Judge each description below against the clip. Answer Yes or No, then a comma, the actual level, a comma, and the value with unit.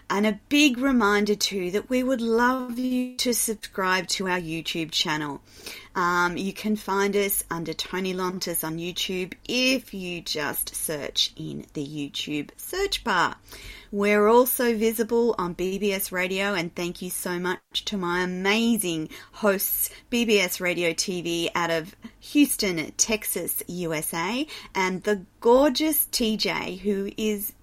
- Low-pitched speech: No, high, 195 Hz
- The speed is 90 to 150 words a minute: Yes, average, 140 wpm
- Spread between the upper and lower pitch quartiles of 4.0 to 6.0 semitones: Yes, average, 4.6 semitones